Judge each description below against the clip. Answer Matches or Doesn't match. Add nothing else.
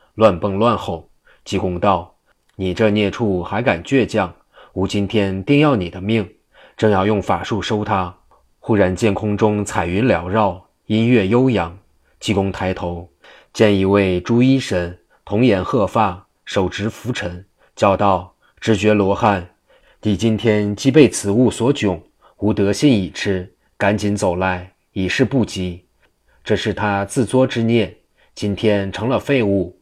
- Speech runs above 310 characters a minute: Doesn't match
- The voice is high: Doesn't match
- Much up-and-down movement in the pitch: Doesn't match